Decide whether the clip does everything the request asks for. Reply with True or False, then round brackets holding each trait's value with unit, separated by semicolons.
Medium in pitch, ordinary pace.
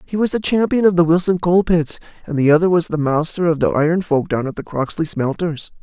False (165 Hz; 245 wpm)